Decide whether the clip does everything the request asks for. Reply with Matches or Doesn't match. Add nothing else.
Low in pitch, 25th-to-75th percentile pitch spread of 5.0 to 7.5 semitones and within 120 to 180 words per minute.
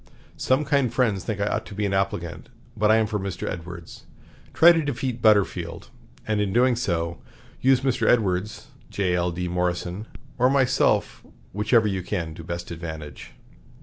Matches